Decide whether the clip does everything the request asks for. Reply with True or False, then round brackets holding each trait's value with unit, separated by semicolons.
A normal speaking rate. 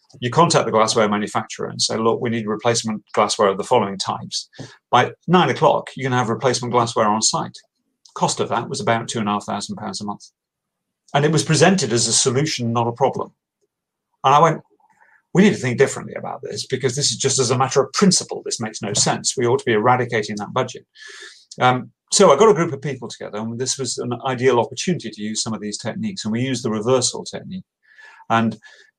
False (220 wpm)